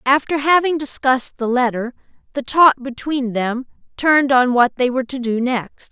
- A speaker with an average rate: Yes, average, 170 wpm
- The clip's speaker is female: Yes, female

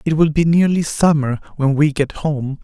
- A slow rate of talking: No, fast, 205 wpm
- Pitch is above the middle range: No, medium, 150 Hz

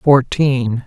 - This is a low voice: Yes, low, 130 Hz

